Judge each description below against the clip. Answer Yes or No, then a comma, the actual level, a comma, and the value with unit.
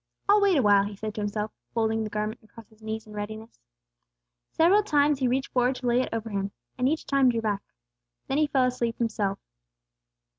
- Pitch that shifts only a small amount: No, average, 3.8 semitones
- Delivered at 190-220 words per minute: Yes, average, 200 wpm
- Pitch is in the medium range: No, high, 230 Hz